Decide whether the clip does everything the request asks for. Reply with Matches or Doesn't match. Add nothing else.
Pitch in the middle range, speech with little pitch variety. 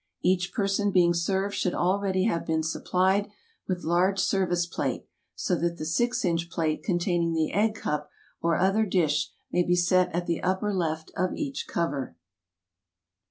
Matches